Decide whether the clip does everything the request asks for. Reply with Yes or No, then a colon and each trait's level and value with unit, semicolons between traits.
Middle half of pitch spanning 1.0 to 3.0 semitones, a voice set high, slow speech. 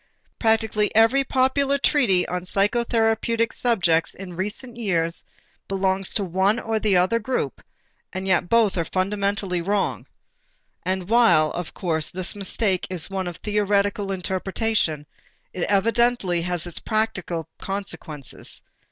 No: average, 3.7 semitones; high, 195 Hz; slow, 130 wpm